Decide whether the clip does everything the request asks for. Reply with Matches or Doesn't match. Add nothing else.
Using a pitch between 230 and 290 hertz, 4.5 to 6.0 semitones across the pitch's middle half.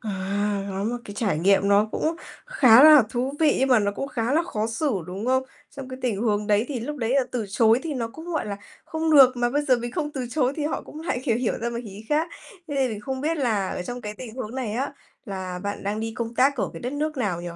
Matches